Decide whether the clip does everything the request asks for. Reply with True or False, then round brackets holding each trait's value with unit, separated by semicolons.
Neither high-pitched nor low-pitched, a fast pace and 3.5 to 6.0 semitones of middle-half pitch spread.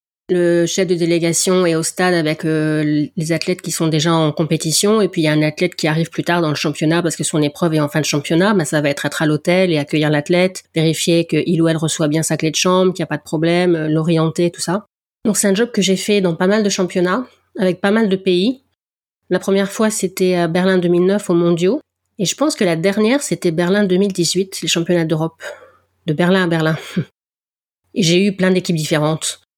False (175 Hz; 235 wpm; 2.7 semitones)